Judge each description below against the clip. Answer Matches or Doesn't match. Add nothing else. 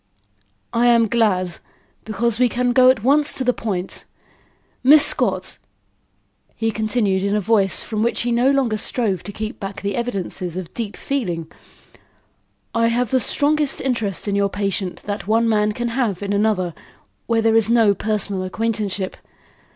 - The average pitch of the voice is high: Matches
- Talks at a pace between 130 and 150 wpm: Doesn't match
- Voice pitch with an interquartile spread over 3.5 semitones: Doesn't match